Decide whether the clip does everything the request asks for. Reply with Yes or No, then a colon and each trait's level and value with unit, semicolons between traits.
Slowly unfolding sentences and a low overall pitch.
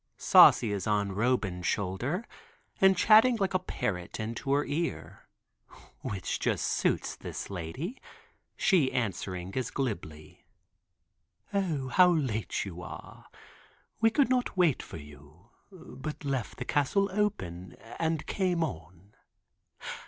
Yes: slow, 125 wpm; low, 130 Hz